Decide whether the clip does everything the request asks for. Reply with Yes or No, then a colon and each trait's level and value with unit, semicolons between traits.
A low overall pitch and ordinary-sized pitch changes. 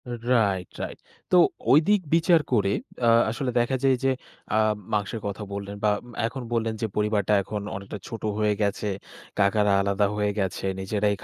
Yes: low, 105 Hz; average, 3.0 semitones